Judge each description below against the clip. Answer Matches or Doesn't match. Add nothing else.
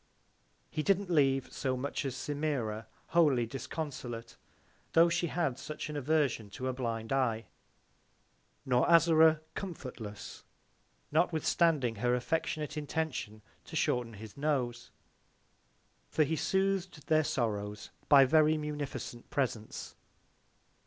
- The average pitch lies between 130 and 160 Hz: Matches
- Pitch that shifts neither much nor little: Matches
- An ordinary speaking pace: Doesn't match